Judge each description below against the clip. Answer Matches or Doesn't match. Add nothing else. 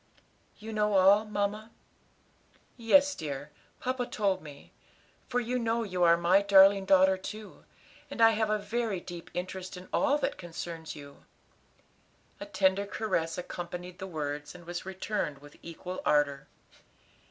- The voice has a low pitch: Doesn't match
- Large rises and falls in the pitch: Doesn't match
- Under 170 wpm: Matches